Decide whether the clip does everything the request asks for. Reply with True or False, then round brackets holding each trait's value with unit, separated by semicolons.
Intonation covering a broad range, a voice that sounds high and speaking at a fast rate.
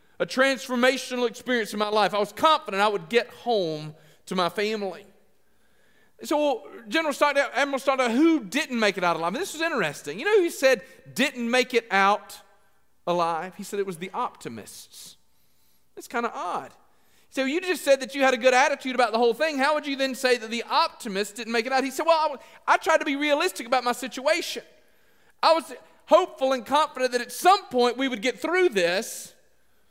True (5.9 semitones; 255 Hz; 210 wpm)